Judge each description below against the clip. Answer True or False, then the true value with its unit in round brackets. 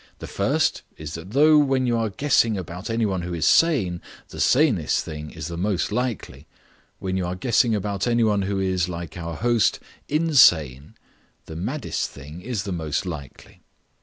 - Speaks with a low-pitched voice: True (95 Hz)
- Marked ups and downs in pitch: True (5.9 semitones)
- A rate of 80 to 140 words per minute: False (180 wpm)